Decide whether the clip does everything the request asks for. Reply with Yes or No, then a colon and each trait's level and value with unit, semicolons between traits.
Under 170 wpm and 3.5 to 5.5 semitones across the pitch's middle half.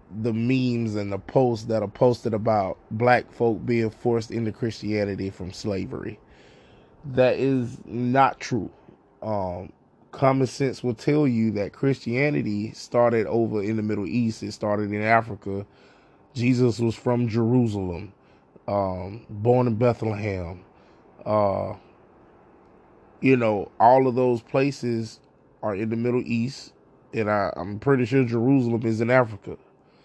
No: slow, 135 wpm; average, 3.0 semitones